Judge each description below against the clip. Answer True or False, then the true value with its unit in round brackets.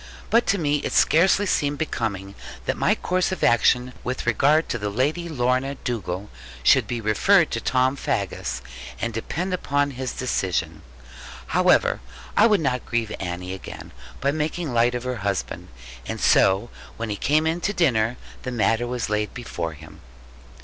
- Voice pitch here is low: True (125 Hz)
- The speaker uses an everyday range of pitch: False (5.8 semitones)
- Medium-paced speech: True (165 wpm)